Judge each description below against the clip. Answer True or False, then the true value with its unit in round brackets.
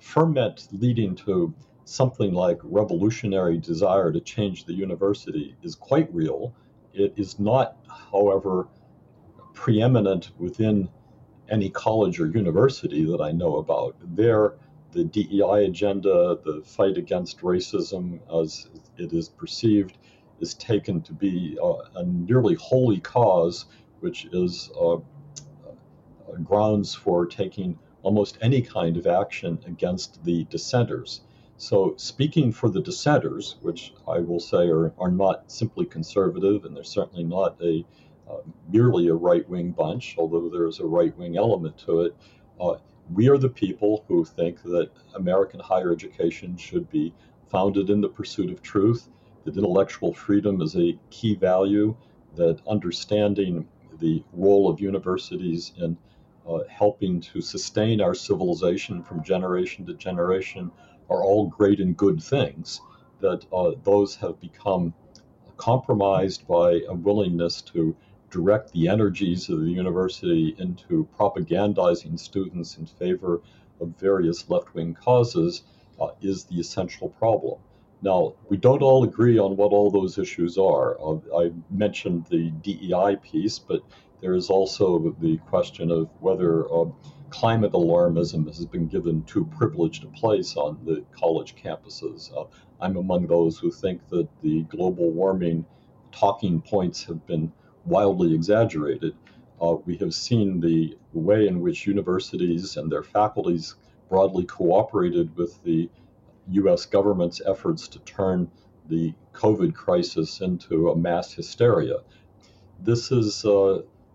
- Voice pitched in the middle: False (95 Hz)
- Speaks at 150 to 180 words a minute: False (140 wpm)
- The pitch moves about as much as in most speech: True (4.3 semitones)